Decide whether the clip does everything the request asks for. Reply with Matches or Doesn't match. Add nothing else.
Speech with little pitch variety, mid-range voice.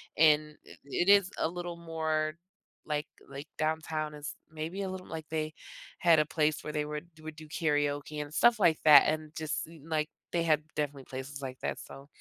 Matches